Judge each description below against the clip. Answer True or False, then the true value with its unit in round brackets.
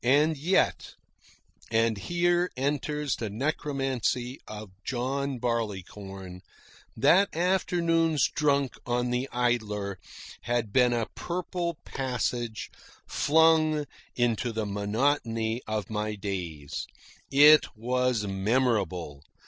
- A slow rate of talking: True (95 wpm)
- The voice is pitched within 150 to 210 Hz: False (125 Hz)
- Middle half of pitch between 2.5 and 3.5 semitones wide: False (5.3 semitones)